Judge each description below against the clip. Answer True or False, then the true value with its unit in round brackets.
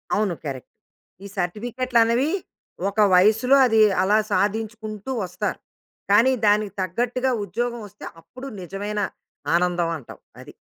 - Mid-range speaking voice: False (210 Hz)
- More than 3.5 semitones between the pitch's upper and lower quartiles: True (3.9 semitones)